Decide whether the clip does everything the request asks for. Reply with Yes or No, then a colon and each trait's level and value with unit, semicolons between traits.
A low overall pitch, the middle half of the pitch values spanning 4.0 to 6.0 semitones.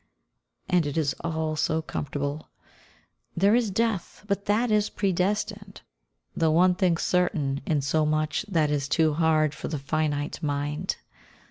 No: medium, 160 Hz; average, 4.3 semitones